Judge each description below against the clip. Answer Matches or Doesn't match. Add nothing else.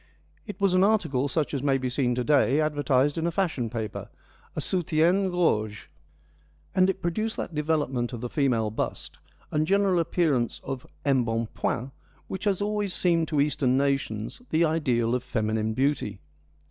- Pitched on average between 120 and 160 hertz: Matches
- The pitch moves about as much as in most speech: Doesn't match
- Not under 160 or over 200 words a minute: Matches